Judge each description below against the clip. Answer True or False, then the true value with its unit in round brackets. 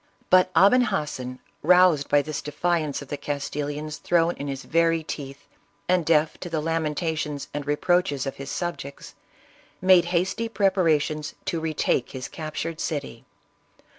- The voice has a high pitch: False (155 Hz)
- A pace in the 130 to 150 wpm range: True (140 wpm)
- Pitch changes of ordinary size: True (3.1 semitones)